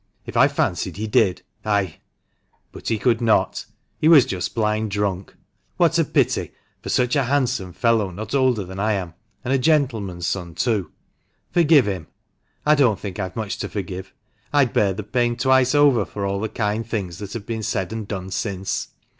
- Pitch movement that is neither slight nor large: Yes, average, 4.2 semitones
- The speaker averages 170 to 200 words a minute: Yes, average, 190 wpm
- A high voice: No, low, 105 Hz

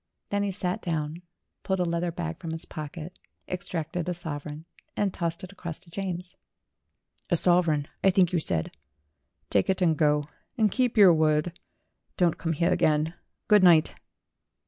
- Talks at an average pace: Yes, average, 165 wpm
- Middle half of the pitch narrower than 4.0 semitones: Yes, average, 2.7 semitones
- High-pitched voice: No, medium, 170 Hz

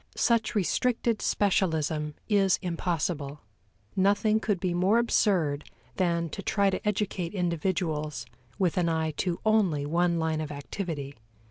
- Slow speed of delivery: Yes, slow, 130 wpm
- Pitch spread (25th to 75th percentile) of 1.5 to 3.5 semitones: No, average, 4.3 semitones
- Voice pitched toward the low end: No, medium, 175 Hz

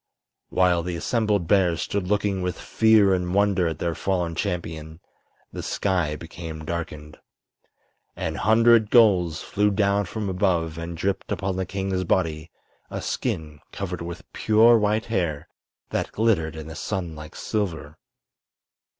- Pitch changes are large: No, average, 3.8 semitones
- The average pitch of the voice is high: No, very low, 90 Hz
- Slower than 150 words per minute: Yes, average, 140 wpm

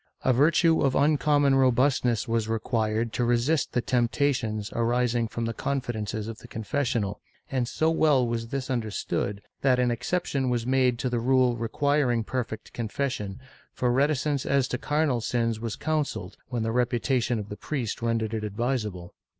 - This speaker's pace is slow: No, average, 165 wpm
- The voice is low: Yes, low, 120 Hz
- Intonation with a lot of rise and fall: No, average, 3.0 semitones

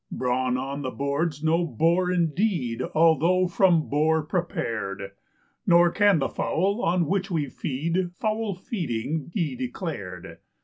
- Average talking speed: No, slow, 130 wpm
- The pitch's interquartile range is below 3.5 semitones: No, average, 4.7 semitones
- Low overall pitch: No, medium, 160 Hz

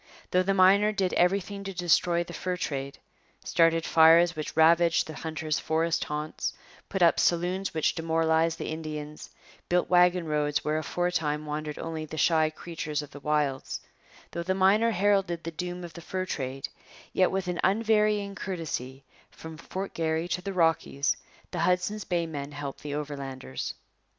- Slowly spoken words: No, average, 165 wpm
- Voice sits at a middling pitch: Yes, medium, 165 Hz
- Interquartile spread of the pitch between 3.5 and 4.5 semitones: No, average, 3.0 semitones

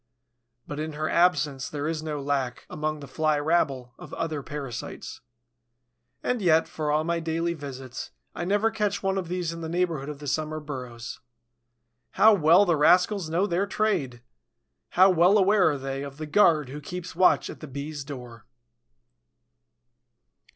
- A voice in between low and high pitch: Yes, medium, 155 Hz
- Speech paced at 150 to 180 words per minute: Yes, average, 165 wpm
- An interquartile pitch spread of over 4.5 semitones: No, average, 3.9 semitones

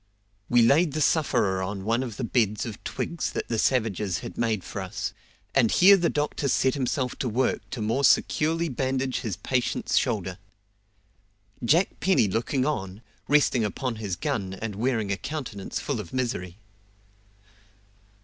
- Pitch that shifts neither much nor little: Yes, average, 4.8 semitones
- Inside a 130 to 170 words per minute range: Yes, average, 160 wpm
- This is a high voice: No, low, 120 Hz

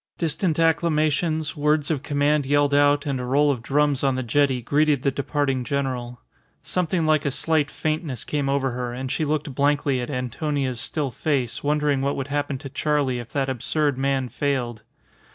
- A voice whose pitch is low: No, medium, 145 Hz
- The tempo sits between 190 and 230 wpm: No, average, 180 wpm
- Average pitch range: No, narrow, 2.2 semitones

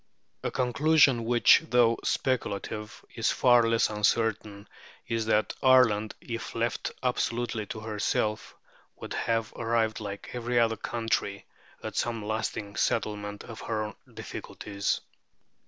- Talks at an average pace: No, slow, 125 wpm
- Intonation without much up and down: Yes, narrow, 1.9 semitones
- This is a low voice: Yes, low, 115 Hz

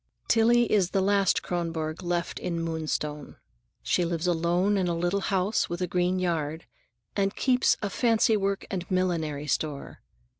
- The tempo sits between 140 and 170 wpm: Yes, average, 150 wpm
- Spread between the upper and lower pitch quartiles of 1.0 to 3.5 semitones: Yes, average, 2.9 semitones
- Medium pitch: Yes, medium, 180 Hz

